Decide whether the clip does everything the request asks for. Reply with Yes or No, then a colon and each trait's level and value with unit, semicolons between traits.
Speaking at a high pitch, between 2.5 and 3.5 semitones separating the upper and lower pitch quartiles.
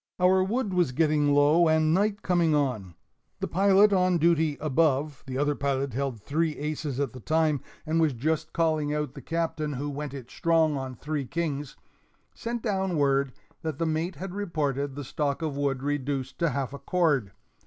No: medium, 150 Hz; average, 3.1 semitones